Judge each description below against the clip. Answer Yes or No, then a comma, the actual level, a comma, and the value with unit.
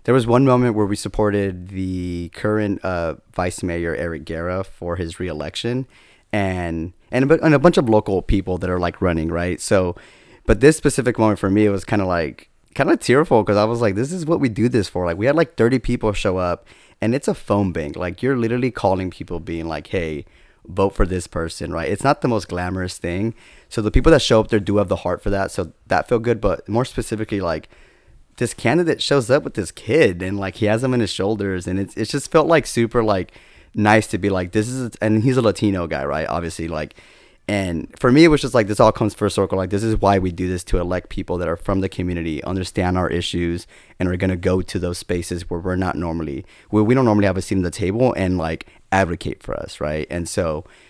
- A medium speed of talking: No, fast, 245 wpm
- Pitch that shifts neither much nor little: Yes, average, 3.9 semitones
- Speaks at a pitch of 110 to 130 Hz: No, very low, 95 Hz